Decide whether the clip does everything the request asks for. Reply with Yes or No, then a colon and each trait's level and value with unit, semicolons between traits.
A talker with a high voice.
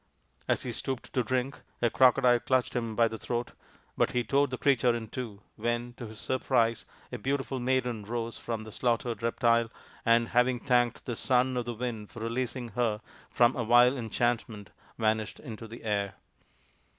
No: low, 120 Hz